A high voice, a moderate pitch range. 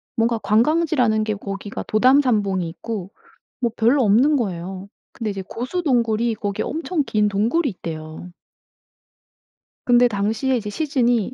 Yes: high, 225 Hz; average, 4.0 semitones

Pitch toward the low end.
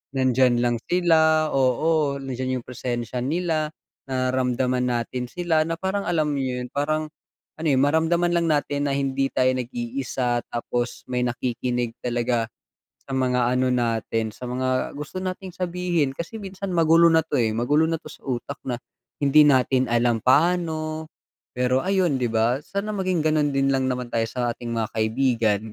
Yes: low, 130 Hz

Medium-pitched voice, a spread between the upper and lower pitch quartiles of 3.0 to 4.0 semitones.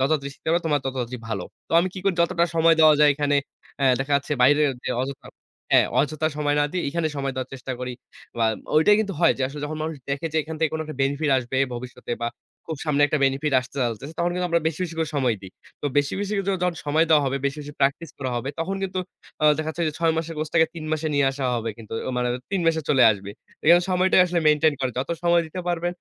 Yes: medium, 150 Hz; average, 3.4 semitones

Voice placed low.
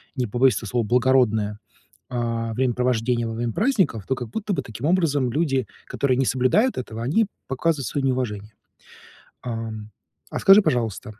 Yes: low, 125 Hz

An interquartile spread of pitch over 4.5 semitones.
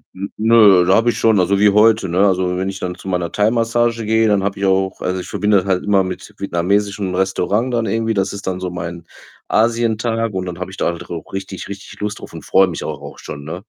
No: average, 2.9 semitones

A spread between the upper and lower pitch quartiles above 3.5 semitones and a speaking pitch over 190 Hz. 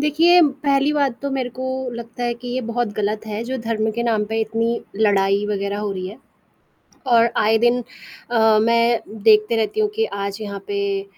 No: average, 2.8 semitones; high, 230 Hz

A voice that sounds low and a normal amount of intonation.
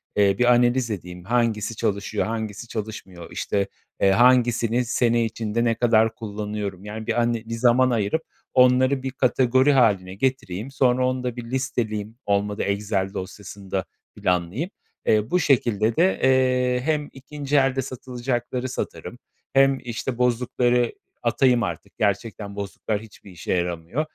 Yes: low, 115 Hz; average, 3.7 semitones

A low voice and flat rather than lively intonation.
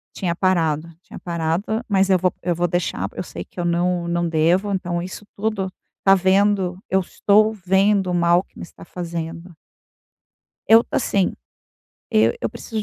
No: medium, 180 Hz; narrow, 2.1 semitones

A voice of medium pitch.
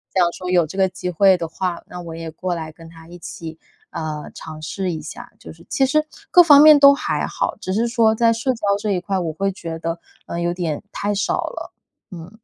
Yes: medium, 180 Hz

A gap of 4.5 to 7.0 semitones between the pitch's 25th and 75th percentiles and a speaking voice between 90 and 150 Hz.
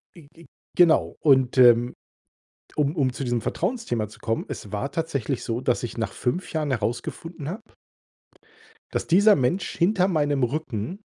Yes: wide, 5.6 semitones; medium, 140 Hz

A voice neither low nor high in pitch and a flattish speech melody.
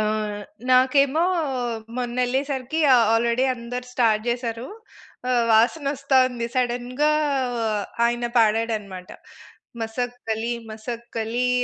No: high, 245 Hz; narrow, 1.9 semitones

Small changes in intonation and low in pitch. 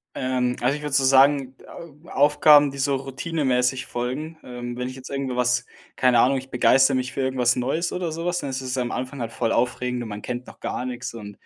Yes: narrow, 1.9 semitones; low, 130 Hz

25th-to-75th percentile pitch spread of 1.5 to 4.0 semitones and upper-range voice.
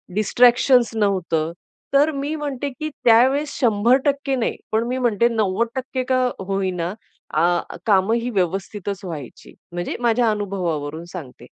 No: wide, 5.4 semitones; high, 220 Hz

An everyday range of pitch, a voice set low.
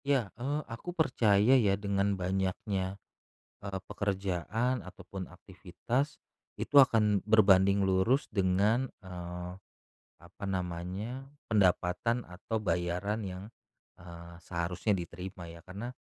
Yes: average, 3.6 semitones; very low, 95 Hz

